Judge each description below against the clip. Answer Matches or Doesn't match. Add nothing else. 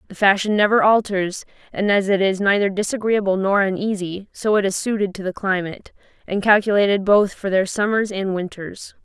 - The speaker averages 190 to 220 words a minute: Doesn't match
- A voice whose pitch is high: Matches